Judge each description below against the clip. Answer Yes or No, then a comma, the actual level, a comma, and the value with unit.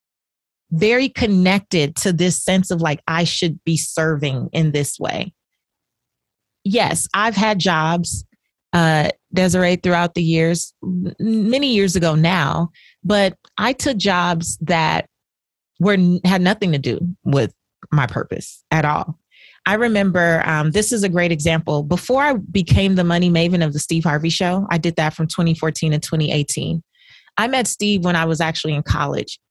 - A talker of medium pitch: Yes, medium, 170 Hz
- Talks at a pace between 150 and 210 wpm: Yes, average, 155 wpm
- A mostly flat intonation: No, average, 3.3 semitones